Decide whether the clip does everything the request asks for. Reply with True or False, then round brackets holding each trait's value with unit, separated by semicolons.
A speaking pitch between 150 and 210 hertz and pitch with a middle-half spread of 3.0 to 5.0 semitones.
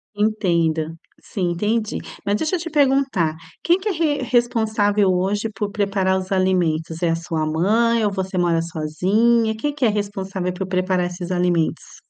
True (195 Hz; 4.1 semitones)